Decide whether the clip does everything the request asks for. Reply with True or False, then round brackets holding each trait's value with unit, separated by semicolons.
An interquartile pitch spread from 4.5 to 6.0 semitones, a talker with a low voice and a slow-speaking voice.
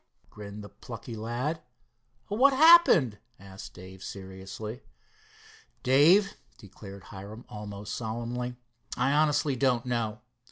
True (5.2 semitones; 115 Hz; 105 wpm)